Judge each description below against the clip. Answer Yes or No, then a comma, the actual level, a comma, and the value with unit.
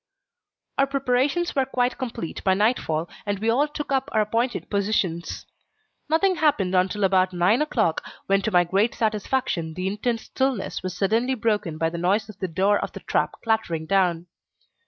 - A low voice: No, high, 210 Hz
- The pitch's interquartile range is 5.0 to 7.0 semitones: Yes, average, 5.3 semitones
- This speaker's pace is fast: No, average, 175 wpm